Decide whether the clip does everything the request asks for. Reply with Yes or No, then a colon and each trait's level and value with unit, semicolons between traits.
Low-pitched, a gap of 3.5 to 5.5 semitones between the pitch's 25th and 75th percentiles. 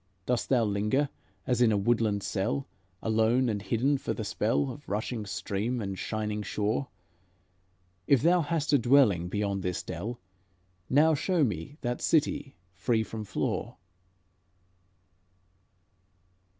Yes: low, 115 Hz; average, 4.6 semitones